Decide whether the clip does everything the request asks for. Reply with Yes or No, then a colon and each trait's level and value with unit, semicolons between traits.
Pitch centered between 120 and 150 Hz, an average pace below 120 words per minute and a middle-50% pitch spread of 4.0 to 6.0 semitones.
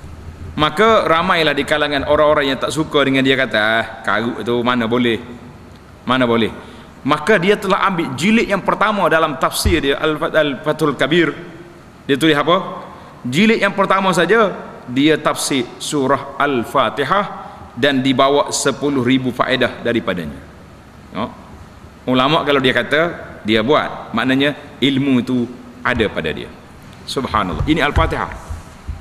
No: medium, 140 Hz; average, 125 wpm; wide, 5.4 semitones